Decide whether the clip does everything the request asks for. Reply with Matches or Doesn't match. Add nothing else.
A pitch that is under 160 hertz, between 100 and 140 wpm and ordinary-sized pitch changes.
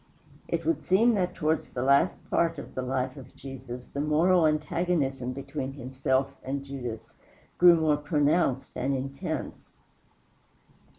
Matches